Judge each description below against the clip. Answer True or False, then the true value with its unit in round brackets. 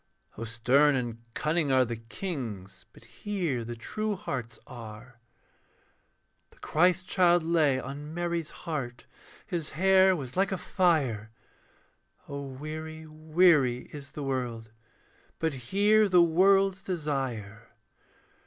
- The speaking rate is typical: False (120 wpm)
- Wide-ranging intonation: True (6.2 semitones)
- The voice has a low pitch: False (150 Hz)